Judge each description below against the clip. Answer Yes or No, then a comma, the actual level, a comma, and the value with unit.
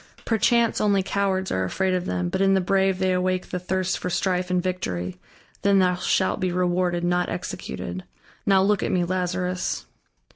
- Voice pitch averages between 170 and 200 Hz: Yes, medium, 185 Hz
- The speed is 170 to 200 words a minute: Yes, average, 180 wpm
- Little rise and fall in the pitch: Yes, narrow, 1.3 semitones